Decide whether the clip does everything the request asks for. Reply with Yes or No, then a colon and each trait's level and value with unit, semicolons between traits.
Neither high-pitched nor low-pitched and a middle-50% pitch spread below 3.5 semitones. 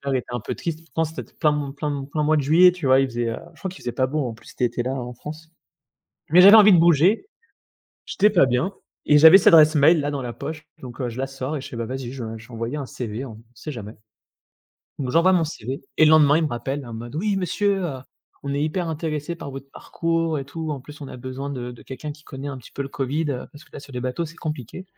No: medium, 145 Hz; average, 4.0 semitones